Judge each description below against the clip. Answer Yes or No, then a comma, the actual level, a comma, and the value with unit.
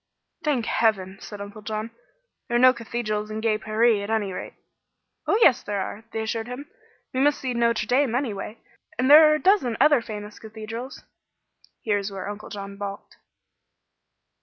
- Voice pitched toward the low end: No, high, 225 Hz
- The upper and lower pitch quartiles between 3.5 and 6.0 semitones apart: No, average, 3.1 semitones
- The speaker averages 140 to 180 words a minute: Yes, average, 175 wpm